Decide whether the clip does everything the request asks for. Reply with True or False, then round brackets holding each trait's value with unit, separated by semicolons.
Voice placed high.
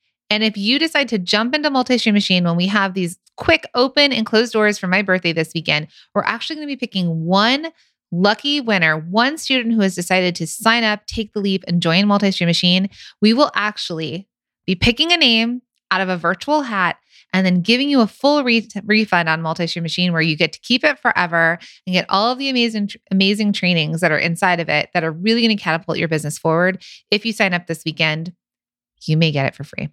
True (195 Hz)